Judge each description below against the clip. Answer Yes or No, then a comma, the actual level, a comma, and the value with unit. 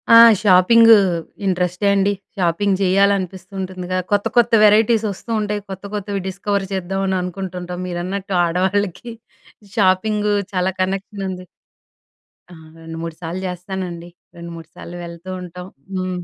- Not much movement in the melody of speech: Yes, narrow, 2.0 semitones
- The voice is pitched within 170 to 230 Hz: Yes, high, 190 Hz